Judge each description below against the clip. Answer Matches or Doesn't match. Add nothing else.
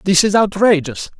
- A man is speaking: Matches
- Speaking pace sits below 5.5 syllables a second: Matches